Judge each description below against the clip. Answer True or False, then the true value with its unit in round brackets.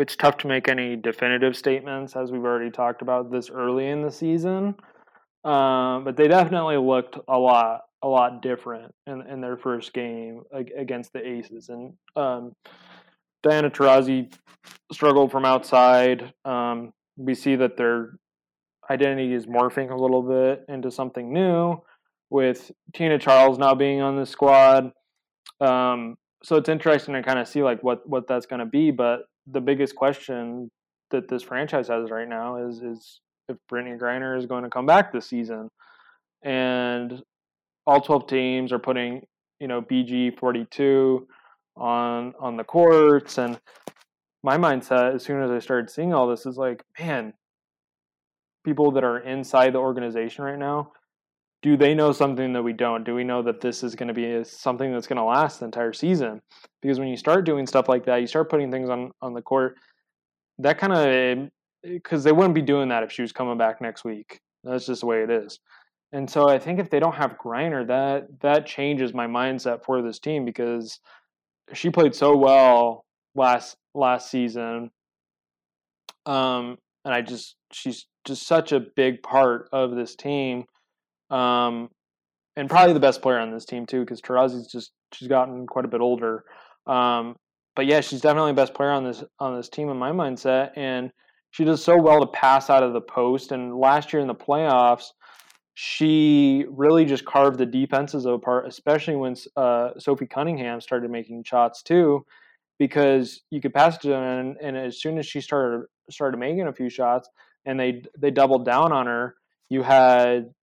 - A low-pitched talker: True (130 Hz)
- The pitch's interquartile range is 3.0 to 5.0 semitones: False (2.4 semitones)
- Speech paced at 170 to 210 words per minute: True (180 wpm)